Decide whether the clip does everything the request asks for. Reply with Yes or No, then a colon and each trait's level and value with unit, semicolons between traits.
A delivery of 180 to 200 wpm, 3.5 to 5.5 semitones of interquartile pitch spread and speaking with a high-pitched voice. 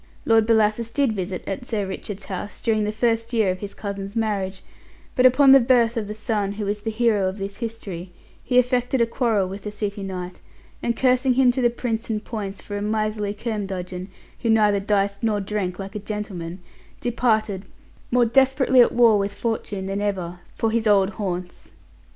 No: average, 190 wpm; average, 2.8 semitones; high, 210 Hz